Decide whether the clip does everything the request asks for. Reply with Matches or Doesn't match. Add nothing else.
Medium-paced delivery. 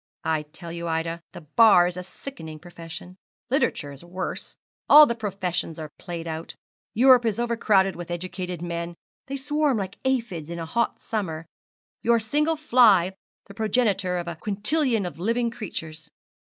Matches